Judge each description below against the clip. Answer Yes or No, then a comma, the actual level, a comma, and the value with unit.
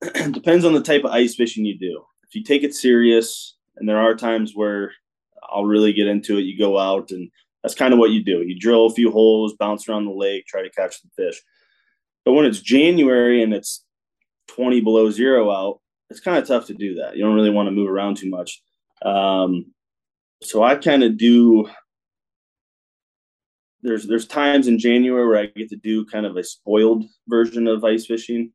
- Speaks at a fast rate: Yes, fast, 210 wpm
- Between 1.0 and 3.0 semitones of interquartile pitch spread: Yes, narrow, 2.6 semitones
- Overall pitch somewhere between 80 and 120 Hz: Yes, low, 110 Hz